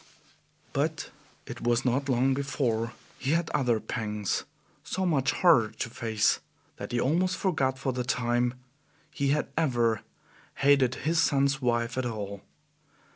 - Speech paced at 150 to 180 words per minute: No, average, 140 wpm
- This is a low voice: Yes, low, 130 Hz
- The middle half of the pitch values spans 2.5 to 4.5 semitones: Yes, average, 3.1 semitones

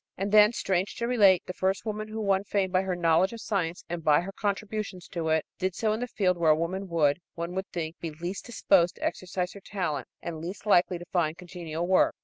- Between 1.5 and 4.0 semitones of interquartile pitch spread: Yes, average, 2.8 semitones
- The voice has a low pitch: No, medium, 185 Hz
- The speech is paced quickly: Yes, fast, 235 wpm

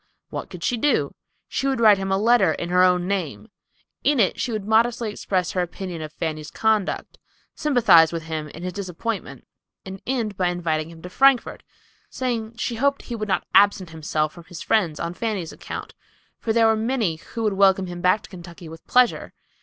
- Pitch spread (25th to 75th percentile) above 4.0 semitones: Yes, average, 4.8 semitones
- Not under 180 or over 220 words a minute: Yes, average, 200 wpm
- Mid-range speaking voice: No, high, 195 Hz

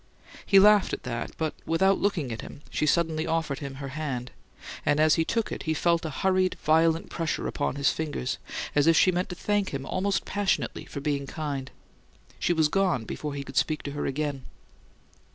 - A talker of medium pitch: Yes, medium, 155 Hz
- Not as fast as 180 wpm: No, average, 200 wpm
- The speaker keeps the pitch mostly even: No, average, 3.8 semitones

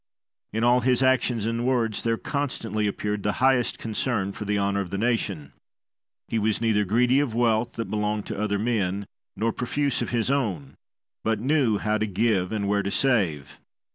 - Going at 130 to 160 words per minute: No, average, 185 wpm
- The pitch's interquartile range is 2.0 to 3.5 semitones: Yes, average, 3.0 semitones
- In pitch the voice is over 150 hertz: No, low, 110 Hz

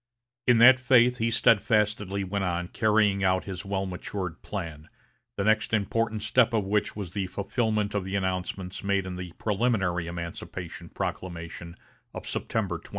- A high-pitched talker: No, low, 100 Hz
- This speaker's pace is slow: No, average, 155 wpm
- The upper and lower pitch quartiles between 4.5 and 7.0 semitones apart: No, average, 3.0 semitones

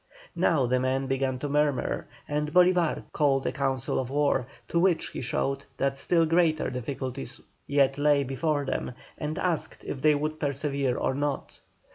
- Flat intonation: Yes, narrow, 2.3 semitones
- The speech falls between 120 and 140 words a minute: No, average, 165 wpm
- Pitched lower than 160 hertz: Yes, medium, 140 Hz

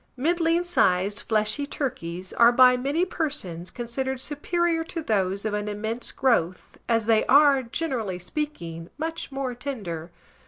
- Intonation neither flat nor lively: No, wide, 6.4 semitones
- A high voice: Yes, high, 245 Hz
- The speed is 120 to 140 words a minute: Yes, slow, 135 wpm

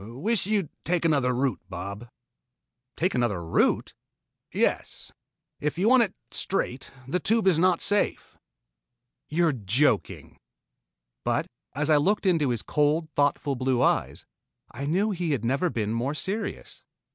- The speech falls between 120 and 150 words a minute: Yes, average, 145 wpm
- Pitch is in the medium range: Yes, medium, 150 Hz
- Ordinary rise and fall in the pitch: No, wide, 6.4 semitones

